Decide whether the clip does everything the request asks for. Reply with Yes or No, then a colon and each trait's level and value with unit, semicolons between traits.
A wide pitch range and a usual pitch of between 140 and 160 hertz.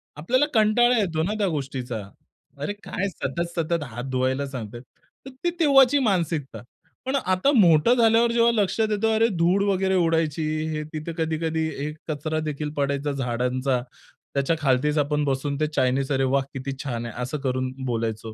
Yes: wide, 6.1 semitones; medium, 155 Hz